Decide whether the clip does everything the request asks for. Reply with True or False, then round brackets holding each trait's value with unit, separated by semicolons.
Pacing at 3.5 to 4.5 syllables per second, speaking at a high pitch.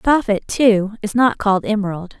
False (5.6 syllables/s; 215 Hz)